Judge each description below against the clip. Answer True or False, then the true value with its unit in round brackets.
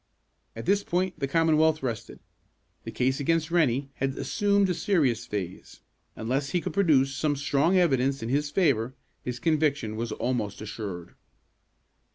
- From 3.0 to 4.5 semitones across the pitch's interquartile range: False (5.3 semitones)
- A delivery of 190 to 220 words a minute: False (150 wpm)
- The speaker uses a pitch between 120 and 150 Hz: True (140 Hz)